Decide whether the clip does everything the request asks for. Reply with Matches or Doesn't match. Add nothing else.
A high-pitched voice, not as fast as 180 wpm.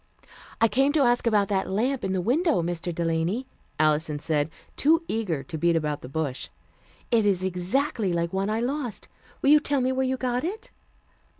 Doesn't match